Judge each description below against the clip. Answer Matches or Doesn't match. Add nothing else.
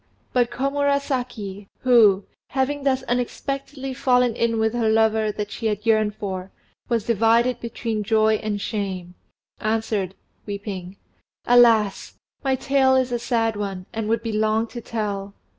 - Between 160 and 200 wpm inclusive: Doesn't match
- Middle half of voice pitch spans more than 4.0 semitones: Doesn't match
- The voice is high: Matches